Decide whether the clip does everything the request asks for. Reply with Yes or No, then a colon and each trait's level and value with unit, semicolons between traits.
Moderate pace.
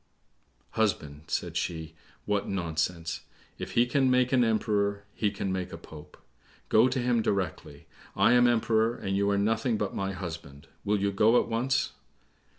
Yes: average, 165 wpm